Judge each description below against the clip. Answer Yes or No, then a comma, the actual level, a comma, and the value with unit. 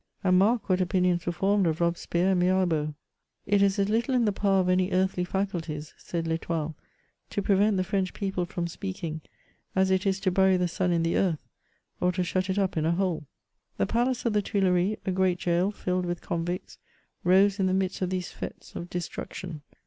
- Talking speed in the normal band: No, fast, 215 wpm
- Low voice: No, medium, 185 Hz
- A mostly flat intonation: Yes, narrow, 1.9 semitones